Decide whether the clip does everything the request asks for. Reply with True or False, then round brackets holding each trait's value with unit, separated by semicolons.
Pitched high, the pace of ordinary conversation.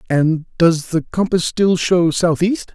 False (170 Hz; 155 wpm)